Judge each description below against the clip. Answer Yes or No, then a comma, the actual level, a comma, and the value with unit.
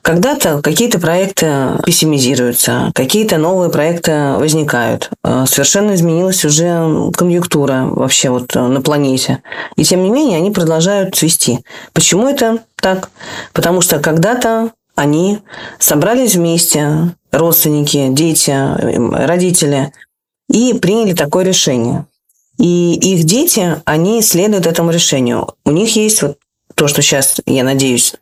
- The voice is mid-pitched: Yes, medium, 165 Hz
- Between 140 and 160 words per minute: No, average, 115 wpm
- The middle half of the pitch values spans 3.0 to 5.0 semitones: Yes, average, 4.6 semitones